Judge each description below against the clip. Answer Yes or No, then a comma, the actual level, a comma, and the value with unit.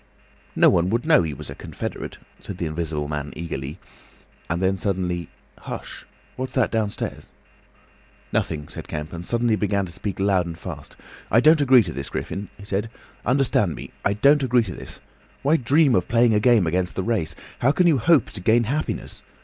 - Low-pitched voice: Yes, low, 100 Hz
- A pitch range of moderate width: No, wide, 6.0 semitones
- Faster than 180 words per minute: Yes, average, 190 wpm